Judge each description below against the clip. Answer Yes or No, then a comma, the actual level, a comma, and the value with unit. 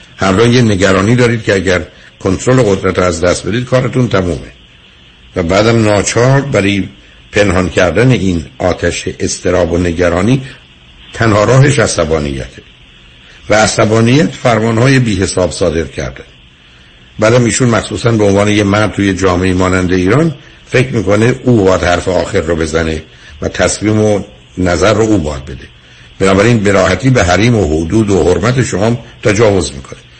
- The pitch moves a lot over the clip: No, average, 4.9 semitones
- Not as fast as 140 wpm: No, average, 145 wpm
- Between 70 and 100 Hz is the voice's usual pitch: Yes, very low, 95 Hz